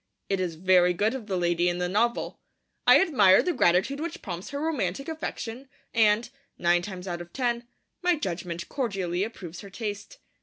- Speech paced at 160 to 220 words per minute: Yes, average, 180 wpm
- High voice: Yes, high, 200 Hz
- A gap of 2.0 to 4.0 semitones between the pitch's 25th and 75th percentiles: No, wide, 5.5 semitones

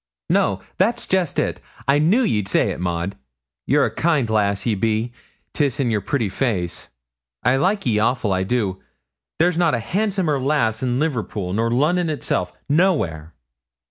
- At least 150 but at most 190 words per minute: Yes, average, 170 wpm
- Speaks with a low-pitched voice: Yes, low, 125 Hz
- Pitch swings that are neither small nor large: No, wide, 7.5 semitones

